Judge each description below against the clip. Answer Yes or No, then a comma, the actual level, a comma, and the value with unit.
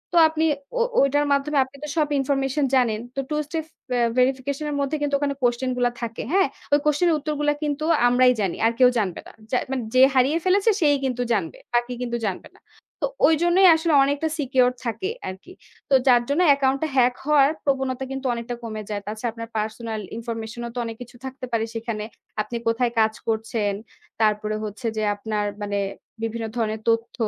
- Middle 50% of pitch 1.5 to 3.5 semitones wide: No, average, 4.0 semitones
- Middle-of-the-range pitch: No, very high, 250 Hz